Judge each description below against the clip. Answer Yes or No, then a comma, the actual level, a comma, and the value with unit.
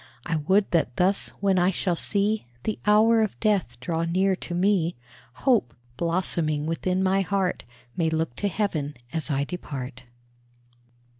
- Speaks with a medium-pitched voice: Yes, medium, 180 Hz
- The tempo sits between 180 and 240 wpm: No, average, 150 wpm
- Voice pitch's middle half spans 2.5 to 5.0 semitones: Yes, average, 3.8 semitones